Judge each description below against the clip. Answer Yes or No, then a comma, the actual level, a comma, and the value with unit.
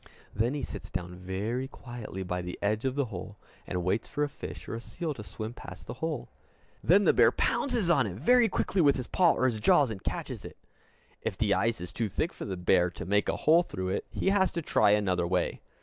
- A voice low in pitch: Yes, low, 110 Hz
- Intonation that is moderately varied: No, wide, 7.5 semitones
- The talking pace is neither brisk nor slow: No, fast, 240 wpm